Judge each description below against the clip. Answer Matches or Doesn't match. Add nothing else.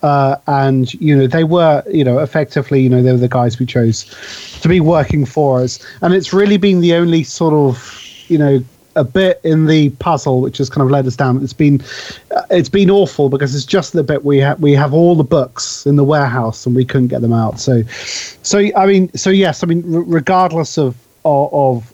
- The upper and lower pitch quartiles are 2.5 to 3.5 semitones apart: Doesn't match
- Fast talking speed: Matches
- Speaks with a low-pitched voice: Doesn't match